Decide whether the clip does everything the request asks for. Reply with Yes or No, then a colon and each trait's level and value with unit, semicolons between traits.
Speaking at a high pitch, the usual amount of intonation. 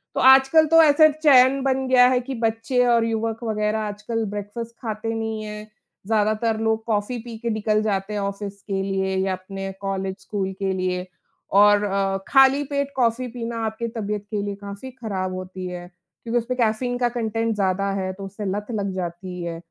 Yes: high, 215 Hz; average, 3.3 semitones